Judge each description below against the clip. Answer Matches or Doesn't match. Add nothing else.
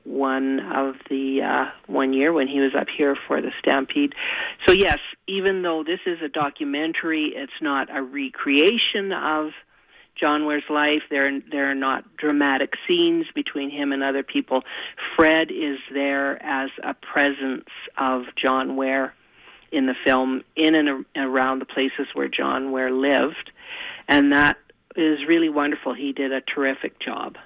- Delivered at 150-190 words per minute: Matches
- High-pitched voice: Doesn't match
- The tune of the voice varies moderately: Doesn't match